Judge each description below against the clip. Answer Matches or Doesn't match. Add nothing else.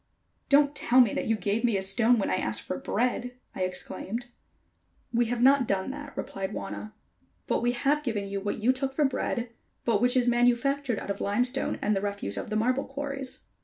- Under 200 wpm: Doesn't match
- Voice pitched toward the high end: Matches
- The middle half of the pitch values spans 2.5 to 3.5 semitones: Doesn't match